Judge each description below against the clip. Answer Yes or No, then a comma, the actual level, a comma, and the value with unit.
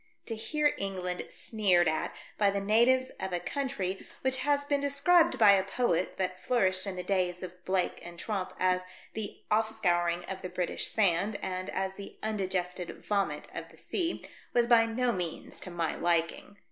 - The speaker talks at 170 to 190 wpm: Yes, average, 185 wpm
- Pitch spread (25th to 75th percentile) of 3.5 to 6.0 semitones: Yes, average, 3.9 semitones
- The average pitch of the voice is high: Yes, high, 195 Hz